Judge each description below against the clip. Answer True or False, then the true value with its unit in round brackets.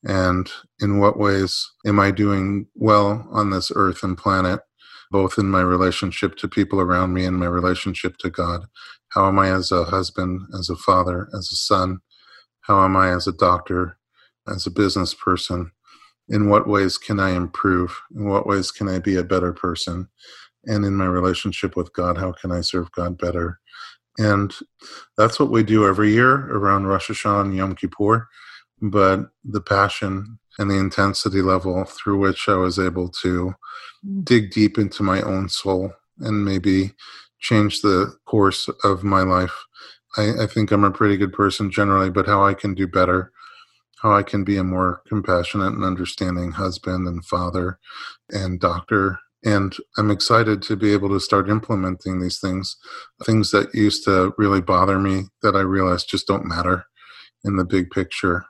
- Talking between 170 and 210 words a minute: True (175 wpm)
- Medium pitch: False (95 Hz)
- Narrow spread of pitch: True (1.9 semitones)